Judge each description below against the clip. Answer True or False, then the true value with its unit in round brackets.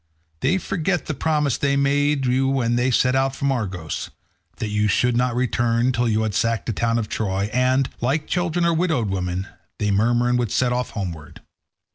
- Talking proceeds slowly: False (195 wpm)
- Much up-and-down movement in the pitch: False (4.1 semitones)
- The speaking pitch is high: False (125 Hz)